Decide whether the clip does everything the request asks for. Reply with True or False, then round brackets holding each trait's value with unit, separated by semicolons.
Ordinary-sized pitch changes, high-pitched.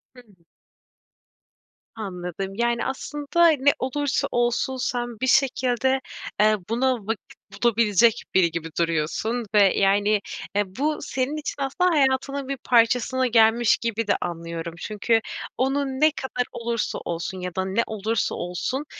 True (4.6 semitones; 235 Hz)